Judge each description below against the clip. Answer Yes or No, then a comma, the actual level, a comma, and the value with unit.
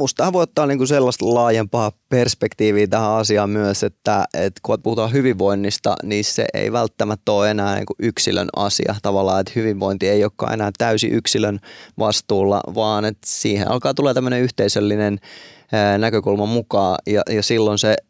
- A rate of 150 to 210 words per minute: Yes, fast, 155 wpm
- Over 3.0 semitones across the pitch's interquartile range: No, narrow, 2.5 semitones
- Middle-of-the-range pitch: No, low, 105 Hz